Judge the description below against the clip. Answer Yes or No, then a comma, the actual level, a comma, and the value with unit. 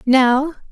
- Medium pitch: No, very high, 270 Hz